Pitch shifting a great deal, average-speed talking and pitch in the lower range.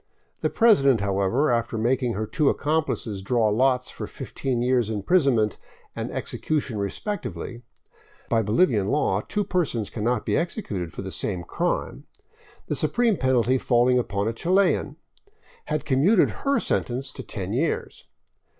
Yes: wide, 6.1 semitones; average, 150 wpm; low, 125 Hz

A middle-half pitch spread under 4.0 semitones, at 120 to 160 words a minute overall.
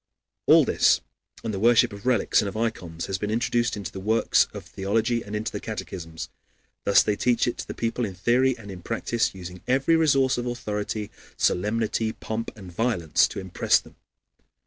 No: average, 3.4 semitones; average, 185 wpm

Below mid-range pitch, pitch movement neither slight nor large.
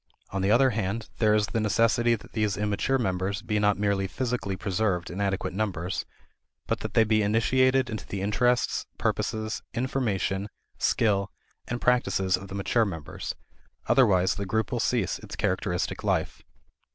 Yes: low, 105 Hz; average, 3.1 semitones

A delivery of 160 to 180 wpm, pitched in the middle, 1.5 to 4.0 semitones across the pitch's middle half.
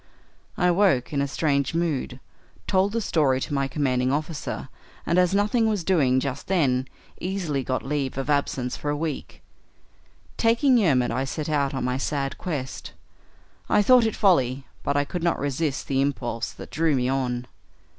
No: average, 175 wpm; medium, 145 Hz; average, 4.9 semitones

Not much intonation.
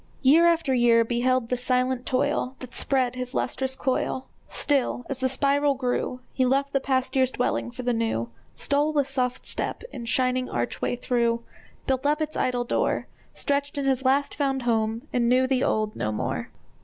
Yes: narrow, 1.9 semitones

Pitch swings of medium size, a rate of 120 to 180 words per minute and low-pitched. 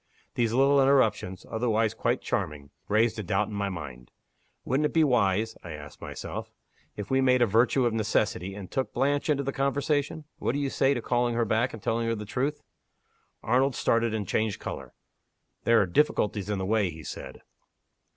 No: average, 4.7 semitones; average, 190 wpm; low, 115 Hz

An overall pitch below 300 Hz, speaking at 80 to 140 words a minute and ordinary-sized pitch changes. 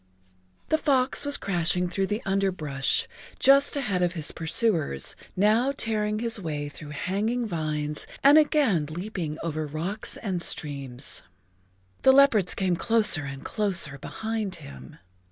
No: medium, 185 Hz; slow, 135 wpm; wide, 6.4 semitones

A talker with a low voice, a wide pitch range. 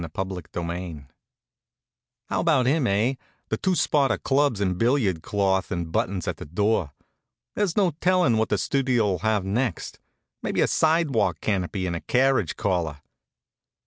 Yes: low, 105 Hz; wide, 6.7 semitones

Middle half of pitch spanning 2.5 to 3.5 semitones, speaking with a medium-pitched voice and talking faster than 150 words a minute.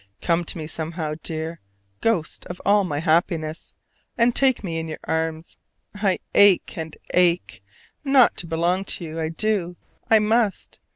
No: average, 4.0 semitones; medium, 170 Hz; average, 160 wpm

